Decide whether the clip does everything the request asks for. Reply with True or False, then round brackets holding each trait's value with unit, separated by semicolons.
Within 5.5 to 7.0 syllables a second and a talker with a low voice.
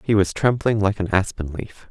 False (5.0 syllables/s; 100 Hz)